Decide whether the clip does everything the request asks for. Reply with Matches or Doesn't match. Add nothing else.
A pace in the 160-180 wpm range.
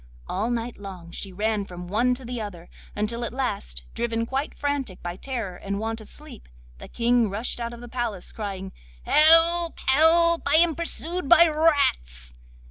Matches